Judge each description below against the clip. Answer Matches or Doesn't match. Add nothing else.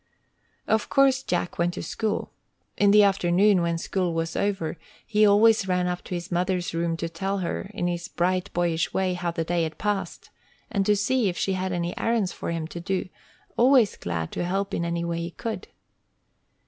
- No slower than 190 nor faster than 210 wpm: Matches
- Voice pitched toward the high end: Doesn't match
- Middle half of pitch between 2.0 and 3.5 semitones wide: Matches